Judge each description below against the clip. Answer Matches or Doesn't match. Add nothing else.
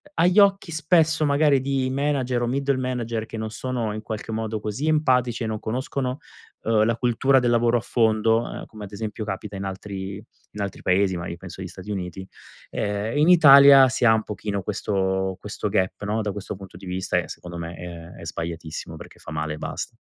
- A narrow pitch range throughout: Doesn't match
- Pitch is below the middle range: Matches